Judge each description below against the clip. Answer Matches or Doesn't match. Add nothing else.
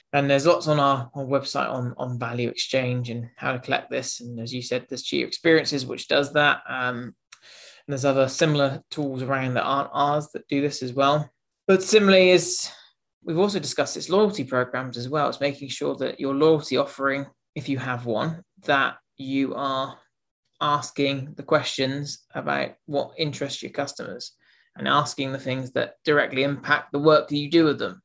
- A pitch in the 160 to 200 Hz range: Doesn't match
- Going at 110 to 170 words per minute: Doesn't match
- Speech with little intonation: Matches